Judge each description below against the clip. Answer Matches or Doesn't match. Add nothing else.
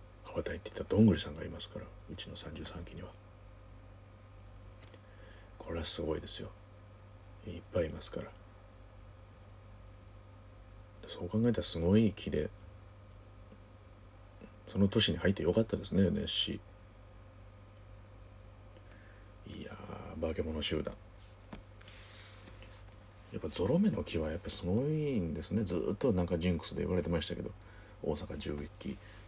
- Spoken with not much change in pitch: Matches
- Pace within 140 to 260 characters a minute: Matches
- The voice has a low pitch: Matches